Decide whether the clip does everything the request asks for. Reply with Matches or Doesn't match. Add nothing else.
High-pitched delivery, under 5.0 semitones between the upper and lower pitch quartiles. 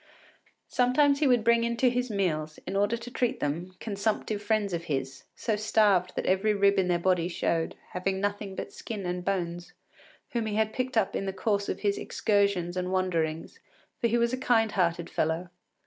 Matches